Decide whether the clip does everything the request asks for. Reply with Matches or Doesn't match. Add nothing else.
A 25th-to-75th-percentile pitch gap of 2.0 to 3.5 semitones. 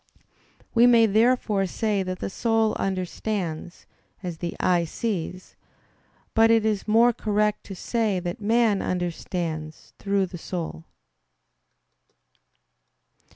Doesn't match